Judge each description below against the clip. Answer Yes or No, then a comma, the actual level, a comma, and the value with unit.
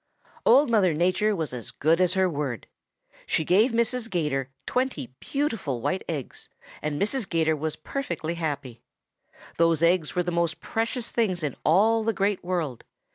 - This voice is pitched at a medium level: Yes, medium, 175 Hz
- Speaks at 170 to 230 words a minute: No, average, 160 wpm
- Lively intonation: Yes, wide, 5.8 semitones